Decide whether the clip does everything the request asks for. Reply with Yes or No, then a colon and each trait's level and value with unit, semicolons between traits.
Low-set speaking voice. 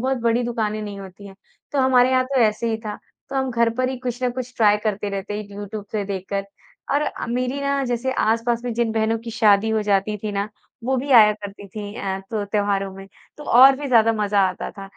No: high, 225 Hz